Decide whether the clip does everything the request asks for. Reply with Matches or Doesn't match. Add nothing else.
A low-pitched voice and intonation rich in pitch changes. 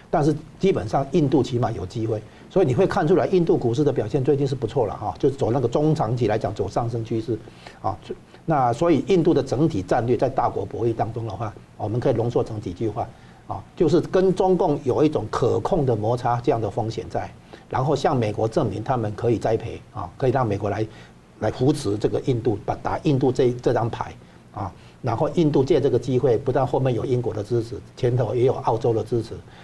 Doesn't match